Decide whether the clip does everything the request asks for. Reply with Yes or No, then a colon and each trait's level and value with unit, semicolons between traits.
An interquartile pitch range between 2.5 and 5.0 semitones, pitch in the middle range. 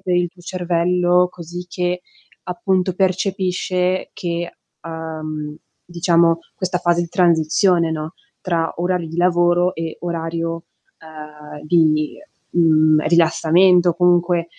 No: narrow, 1.7 semitones; medium, 175 Hz